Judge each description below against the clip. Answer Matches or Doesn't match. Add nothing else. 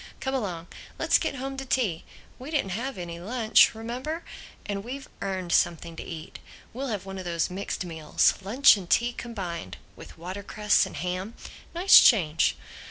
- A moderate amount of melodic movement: Doesn't match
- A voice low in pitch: Doesn't match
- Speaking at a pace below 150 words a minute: Doesn't match